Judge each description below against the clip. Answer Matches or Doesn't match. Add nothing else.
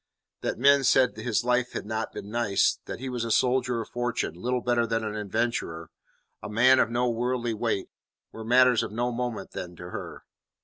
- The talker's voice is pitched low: Matches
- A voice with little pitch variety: Matches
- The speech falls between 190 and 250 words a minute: Matches